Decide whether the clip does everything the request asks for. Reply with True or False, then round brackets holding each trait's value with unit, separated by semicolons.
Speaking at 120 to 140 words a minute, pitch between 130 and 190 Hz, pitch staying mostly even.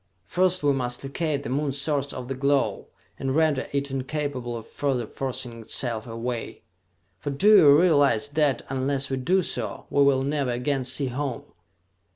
False (170 wpm; 140 Hz; 2.1 semitones)